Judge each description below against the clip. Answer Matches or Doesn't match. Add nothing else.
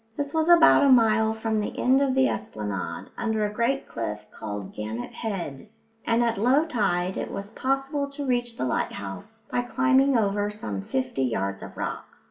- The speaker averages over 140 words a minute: Matches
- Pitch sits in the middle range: Doesn't match